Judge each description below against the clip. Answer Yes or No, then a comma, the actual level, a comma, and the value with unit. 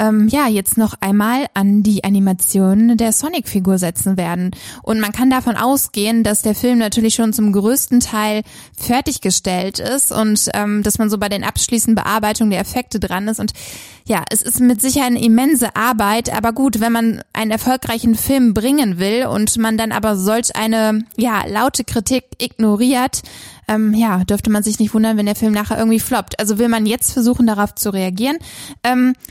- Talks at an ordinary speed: Yes, average, 180 wpm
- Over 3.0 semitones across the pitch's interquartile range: No, narrow, 2.5 semitones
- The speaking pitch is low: No, high, 220 Hz